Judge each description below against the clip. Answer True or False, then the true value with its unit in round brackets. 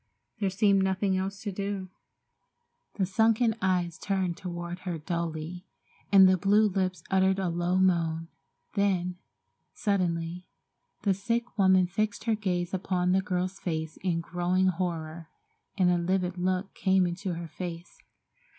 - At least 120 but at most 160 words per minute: True (140 wpm)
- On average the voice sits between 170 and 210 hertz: True (185 Hz)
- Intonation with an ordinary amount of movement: False (1.9 semitones)